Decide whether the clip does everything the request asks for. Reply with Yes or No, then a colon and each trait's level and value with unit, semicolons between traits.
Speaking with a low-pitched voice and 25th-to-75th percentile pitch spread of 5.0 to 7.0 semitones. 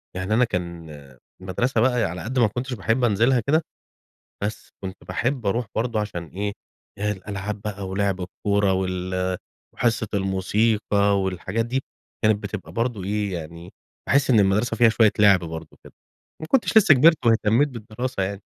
No: low, 105 Hz; average, 3.8 semitones